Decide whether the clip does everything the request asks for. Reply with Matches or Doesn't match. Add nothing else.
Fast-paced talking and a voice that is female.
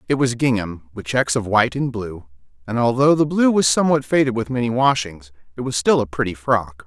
Doesn't match